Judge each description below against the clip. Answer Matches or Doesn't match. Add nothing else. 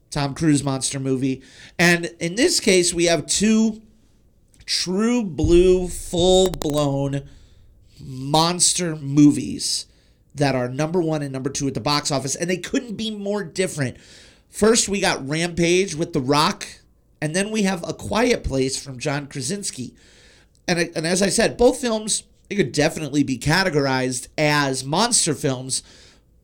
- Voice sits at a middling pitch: Matches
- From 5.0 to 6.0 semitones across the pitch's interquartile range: Matches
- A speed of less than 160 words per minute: Matches